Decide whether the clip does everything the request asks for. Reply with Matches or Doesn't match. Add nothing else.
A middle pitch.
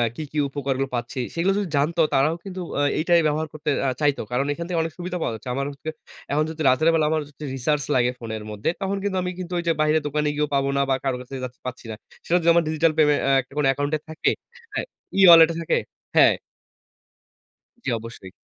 Matches